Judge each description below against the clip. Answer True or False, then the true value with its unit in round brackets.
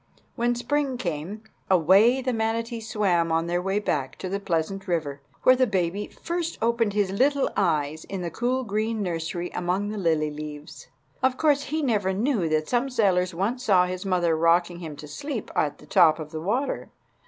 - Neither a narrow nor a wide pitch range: False (5.8 semitones)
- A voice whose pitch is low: False (195 Hz)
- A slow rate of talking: False (190 wpm)